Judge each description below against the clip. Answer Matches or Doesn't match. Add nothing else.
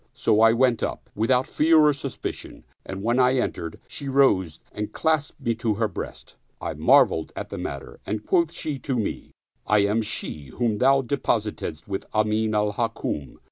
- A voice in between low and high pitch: Doesn't match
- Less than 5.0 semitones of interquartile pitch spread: Matches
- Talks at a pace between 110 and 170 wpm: Doesn't match